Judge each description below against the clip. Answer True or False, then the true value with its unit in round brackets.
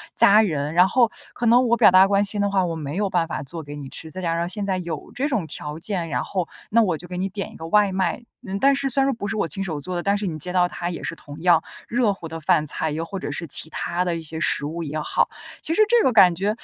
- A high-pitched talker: False (180 Hz)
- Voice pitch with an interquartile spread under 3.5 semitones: False (3.8 semitones)